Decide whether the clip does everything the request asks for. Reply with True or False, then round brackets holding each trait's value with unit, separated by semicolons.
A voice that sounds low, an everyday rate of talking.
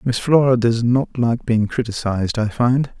True (120 Hz; 180 wpm)